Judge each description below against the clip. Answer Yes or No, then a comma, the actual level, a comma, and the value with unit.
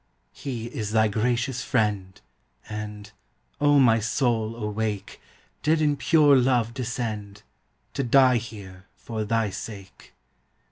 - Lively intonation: No, average, 3.2 semitones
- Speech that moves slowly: Yes, slow, 120 wpm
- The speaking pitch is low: Yes, low, 115 Hz